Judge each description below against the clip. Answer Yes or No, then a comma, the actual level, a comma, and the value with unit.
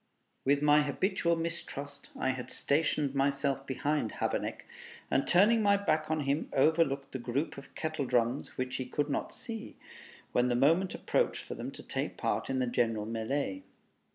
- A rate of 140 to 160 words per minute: No, average, 170 wpm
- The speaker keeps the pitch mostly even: No, average, 3.4 semitones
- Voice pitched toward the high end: No, medium, 140 Hz